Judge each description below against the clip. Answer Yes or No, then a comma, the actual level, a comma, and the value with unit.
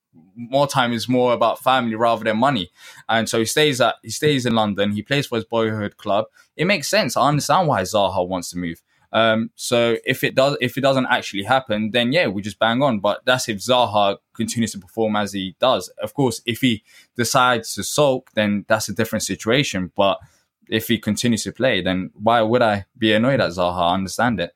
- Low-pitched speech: Yes, low, 115 Hz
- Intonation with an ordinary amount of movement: Yes, average, 3.5 semitones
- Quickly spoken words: Yes, fast, 220 wpm